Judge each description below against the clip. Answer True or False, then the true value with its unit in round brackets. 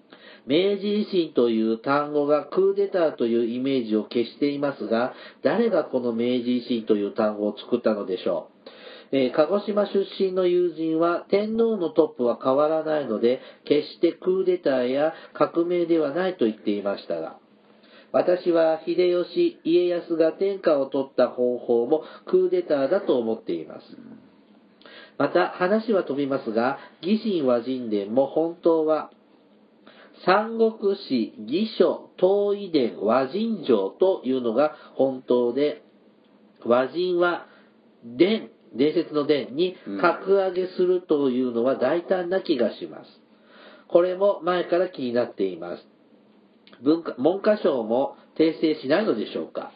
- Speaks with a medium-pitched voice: True (160 Hz)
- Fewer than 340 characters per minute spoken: True (270 characters per minute)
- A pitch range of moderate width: False (6.6 semitones)